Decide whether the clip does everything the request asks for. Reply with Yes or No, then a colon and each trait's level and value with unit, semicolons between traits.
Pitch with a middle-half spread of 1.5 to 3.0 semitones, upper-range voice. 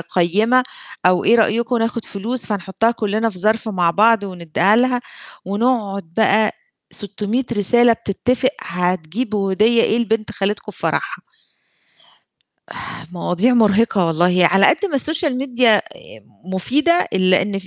No: average, 3.9 semitones; high, 215 Hz